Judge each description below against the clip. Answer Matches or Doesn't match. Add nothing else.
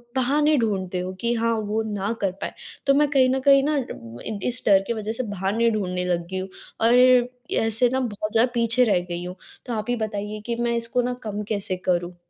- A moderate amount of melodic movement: Matches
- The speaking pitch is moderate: Doesn't match